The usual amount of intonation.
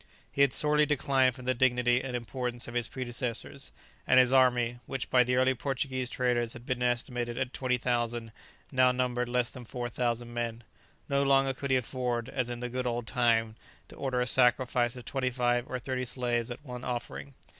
No: narrow, 1.2 semitones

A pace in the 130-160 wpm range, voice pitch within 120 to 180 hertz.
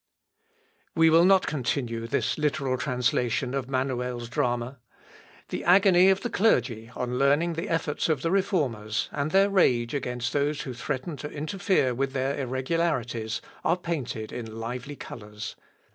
Yes: average, 145 wpm; low, 135 Hz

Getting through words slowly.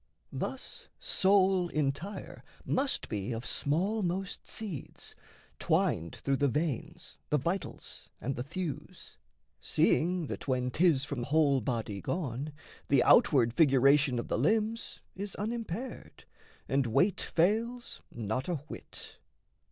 Yes: slow, 120 wpm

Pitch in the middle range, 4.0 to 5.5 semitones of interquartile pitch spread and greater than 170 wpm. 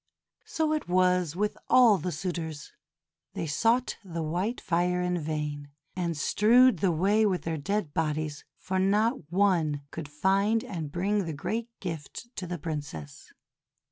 No: medium, 180 Hz; average, 4.7 semitones; average, 150 wpm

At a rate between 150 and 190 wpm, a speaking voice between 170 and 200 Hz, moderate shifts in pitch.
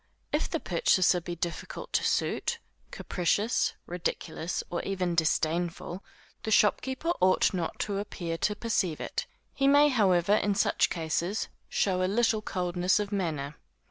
No: average, 140 wpm; medium, 185 Hz; average, 3.3 semitones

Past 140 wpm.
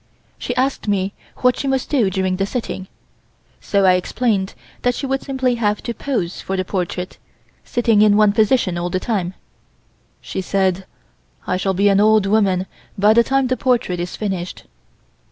Yes: average, 175 wpm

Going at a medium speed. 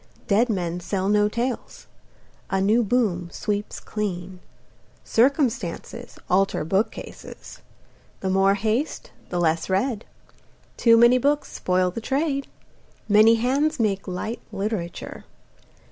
No: slow, 115 wpm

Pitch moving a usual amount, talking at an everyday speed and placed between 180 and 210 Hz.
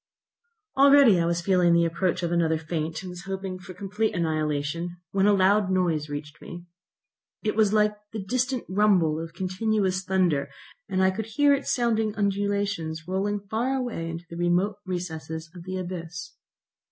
Yes: average, 3.4 semitones; average, 165 wpm; medium, 185 Hz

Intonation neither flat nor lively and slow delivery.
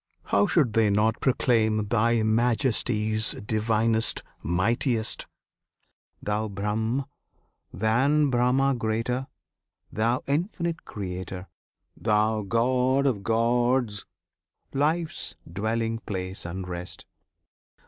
Yes: average, 3.0 semitones; slow, 85 wpm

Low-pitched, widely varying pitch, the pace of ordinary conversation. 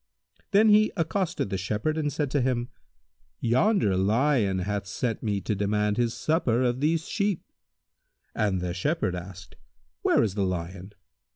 Yes: low, 115 Hz; wide, 7.7 semitones; average, 150 wpm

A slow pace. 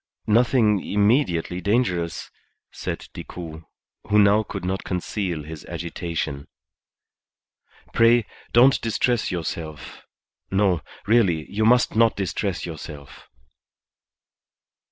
Yes: slow, 95 wpm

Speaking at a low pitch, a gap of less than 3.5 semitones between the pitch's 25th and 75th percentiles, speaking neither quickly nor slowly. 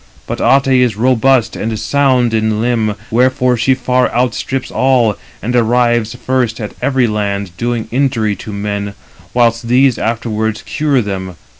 Yes: low, 120 Hz; average, 2.8 semitones; average, 145 wpm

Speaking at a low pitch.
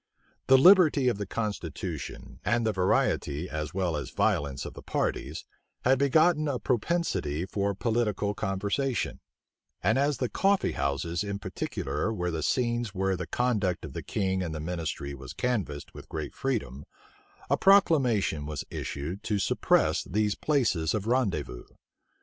Yes: low, 100 Hz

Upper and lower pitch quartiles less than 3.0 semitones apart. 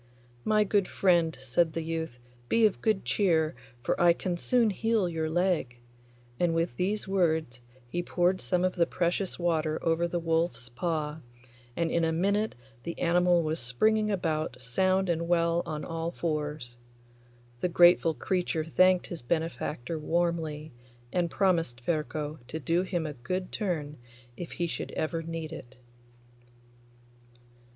Yes: narrow, 2.4 semitones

